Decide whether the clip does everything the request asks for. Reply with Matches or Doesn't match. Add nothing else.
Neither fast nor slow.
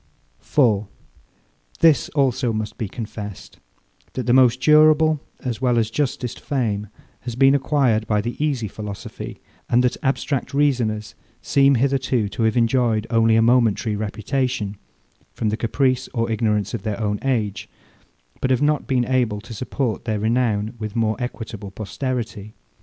Matches